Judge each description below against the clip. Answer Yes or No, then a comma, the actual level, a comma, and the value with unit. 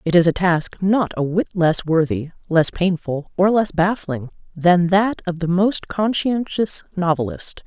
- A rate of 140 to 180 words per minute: Yes, average, 165 wpm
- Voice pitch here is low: No, medium, 175 Hz